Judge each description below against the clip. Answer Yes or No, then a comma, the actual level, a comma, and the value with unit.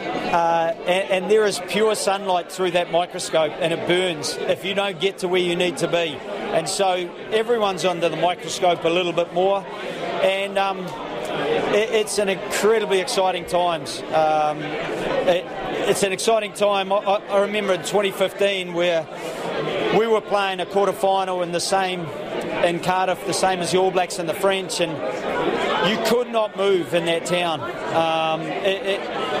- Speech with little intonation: Yes, narrow, 2.3 semitones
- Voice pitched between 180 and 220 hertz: Yes, medium, 185 Hz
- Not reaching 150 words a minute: No, average, 170 wpm